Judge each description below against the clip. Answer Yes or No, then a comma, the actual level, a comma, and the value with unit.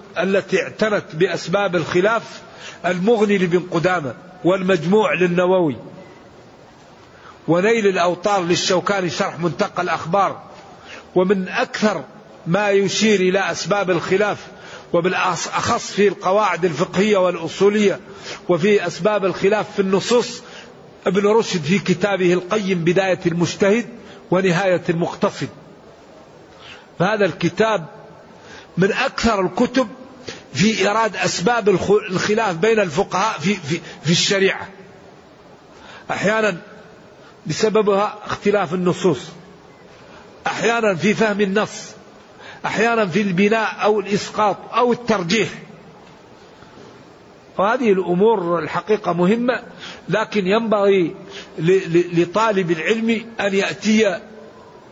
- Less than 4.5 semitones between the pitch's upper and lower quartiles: Yes, average, 2.8 semitones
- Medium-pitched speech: No, high, 200 Hz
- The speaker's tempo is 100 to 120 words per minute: No, average, 85 wpm